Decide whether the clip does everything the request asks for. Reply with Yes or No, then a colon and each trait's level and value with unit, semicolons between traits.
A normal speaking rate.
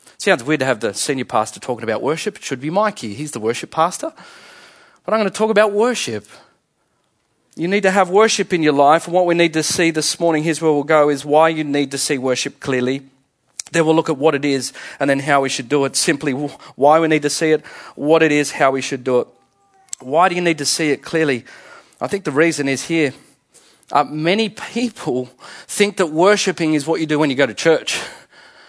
No: fast, 230 wpm